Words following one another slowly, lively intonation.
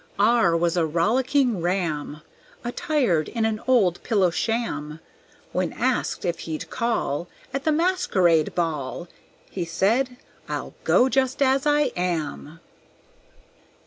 Yes: slow, 120 wpm; wide, 7.4 semitones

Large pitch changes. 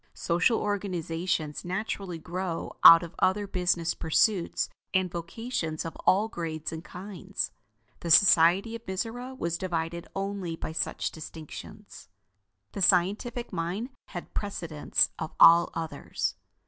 No: average, 3.2 semitones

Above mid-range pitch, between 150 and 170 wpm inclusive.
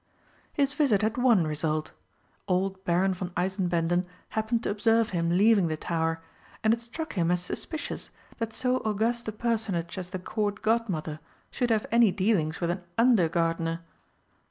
Yes: high, 195 Hz; average, 160 wpm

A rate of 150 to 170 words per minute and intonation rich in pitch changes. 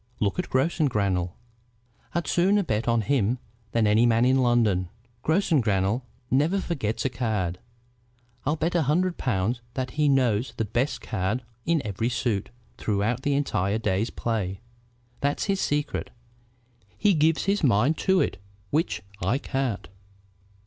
No: average, 140 wpm; wide, 6.1 semitones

